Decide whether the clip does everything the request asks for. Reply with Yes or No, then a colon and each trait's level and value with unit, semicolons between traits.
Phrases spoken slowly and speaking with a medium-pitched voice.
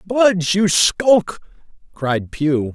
Yes: slow, 110 wpm; medium, 175 Hz